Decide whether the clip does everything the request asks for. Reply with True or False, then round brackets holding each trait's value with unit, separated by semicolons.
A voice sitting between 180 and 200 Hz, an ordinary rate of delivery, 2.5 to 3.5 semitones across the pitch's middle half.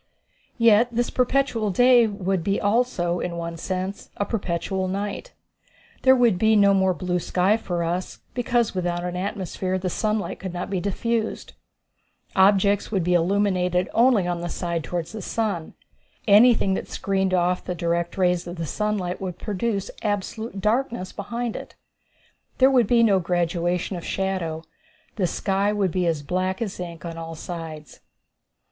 True (190 Hz; 160 wpm; 3.2 semitones)